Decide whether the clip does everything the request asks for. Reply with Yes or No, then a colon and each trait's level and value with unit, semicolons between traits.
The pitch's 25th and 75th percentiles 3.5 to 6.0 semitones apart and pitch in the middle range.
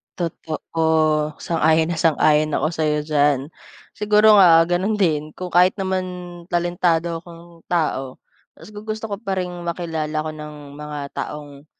No: average, 2.8 semitones; medium, 165 Hz